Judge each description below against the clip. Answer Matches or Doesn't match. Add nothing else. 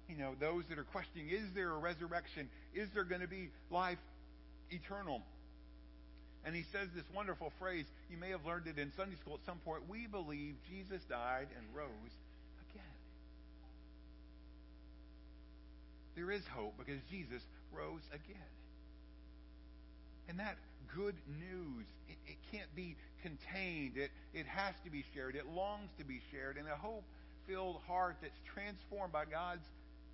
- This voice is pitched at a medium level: Matches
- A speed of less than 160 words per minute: Matches